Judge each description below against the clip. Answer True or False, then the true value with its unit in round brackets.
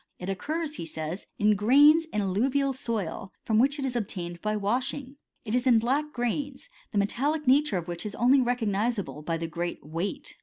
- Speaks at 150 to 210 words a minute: True (195 wpm)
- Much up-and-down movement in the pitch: True (6.0 semitones)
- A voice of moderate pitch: False (230 Hz)